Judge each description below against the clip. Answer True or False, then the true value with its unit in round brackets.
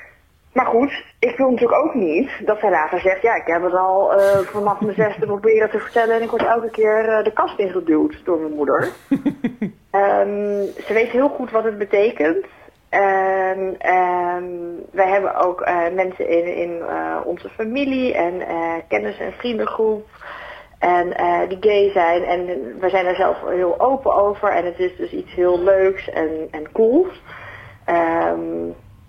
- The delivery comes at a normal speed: True (175 wpm)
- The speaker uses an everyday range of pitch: True (3.8 semitones)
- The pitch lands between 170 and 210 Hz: True (190 Hz)